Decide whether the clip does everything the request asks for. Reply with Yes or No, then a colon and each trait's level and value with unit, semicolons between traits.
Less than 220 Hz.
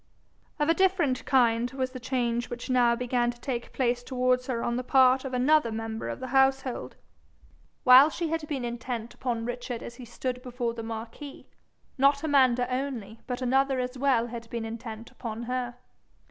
No: very high, 250 Hz